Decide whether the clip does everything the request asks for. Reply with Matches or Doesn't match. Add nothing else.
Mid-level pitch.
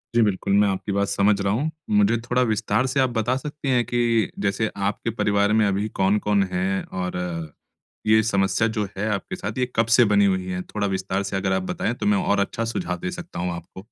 Doesn't match